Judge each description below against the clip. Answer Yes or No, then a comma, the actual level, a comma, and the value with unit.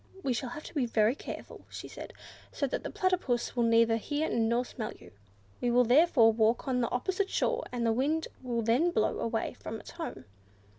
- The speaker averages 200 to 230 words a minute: Yes, fast, 205 wpm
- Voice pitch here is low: No, high, 245 Hz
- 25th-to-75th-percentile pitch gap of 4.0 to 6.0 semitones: Yes, average, 4.5 semitones